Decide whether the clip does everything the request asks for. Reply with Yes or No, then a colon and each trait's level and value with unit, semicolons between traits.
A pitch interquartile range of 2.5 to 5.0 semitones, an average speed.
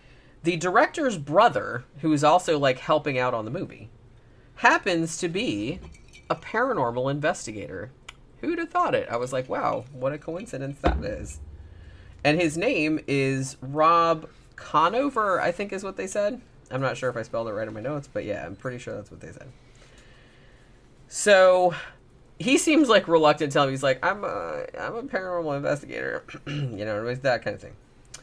No: wide, 5.4 semitones; average, 185 wpm